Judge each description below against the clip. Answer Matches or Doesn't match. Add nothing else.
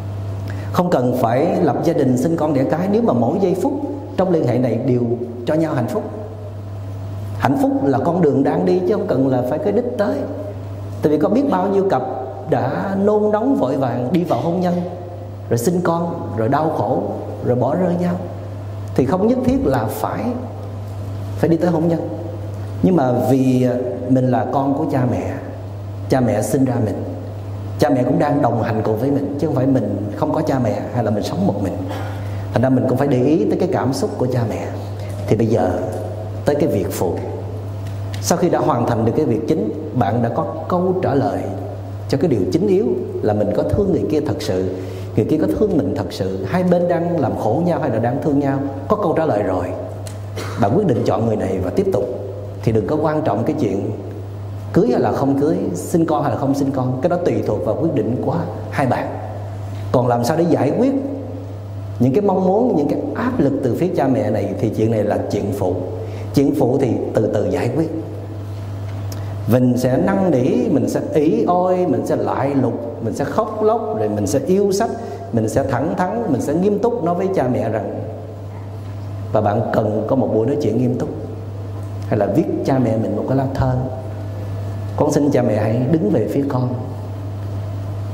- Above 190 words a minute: Matches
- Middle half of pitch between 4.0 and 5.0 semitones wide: Doesn't match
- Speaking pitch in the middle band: Doesn't match